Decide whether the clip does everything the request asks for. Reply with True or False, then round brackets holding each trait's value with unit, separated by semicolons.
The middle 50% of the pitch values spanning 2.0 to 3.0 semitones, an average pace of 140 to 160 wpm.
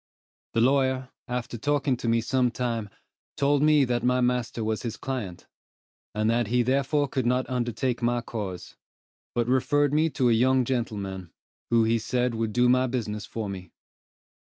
False (2.4 semitones; 170 wpm)